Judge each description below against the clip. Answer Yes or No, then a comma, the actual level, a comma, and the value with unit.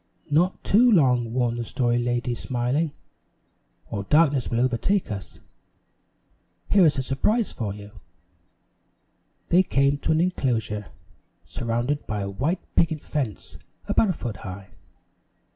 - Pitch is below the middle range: Yes, low, 130 Hz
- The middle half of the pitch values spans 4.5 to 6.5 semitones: Yes, average, 5.3 semitones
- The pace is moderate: No, slow, 130 wpm